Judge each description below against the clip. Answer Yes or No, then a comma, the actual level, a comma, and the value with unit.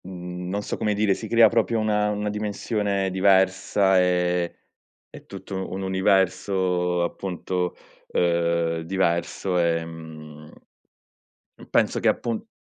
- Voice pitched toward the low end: Yes, very low, 95 Hz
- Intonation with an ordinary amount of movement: No, narrow, 2.2 semitones